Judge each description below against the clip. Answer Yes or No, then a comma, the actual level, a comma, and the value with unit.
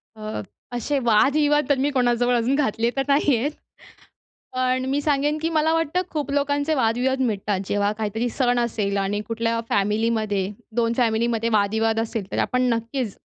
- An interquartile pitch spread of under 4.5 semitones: Yes, average, 4.1 semitones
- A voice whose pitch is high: Yes, high, 235 Hz